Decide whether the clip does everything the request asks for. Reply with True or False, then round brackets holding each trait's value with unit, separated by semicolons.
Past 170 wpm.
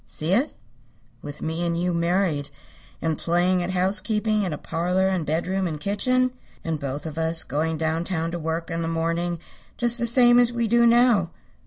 True (190 wpm)